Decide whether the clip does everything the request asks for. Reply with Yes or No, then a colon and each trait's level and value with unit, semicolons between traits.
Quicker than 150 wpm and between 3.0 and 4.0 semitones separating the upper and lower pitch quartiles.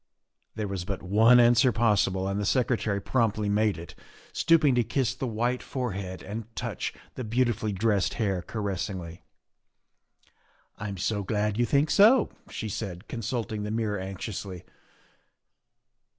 No: average, 140 wpm; average, 3.4 semitones